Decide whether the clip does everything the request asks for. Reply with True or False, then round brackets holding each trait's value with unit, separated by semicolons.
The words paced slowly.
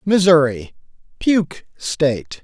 True (75 wpm)